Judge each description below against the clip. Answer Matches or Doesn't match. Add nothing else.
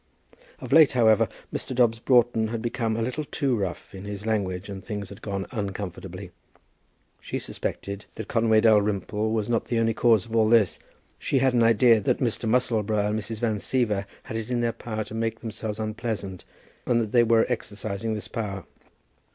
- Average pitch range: Doesn't match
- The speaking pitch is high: Doesn't match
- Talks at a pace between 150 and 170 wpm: Doesn't match